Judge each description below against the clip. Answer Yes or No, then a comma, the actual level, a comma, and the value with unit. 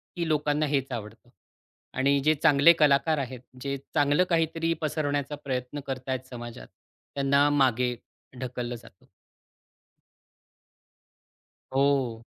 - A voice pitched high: No, medium, 140 Hz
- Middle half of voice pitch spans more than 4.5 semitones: No, average, 2.7 semitones